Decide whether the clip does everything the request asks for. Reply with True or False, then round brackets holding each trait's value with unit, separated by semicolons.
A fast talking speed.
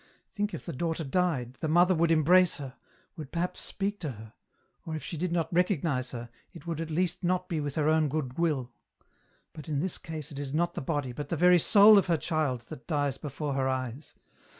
True (220 wpm)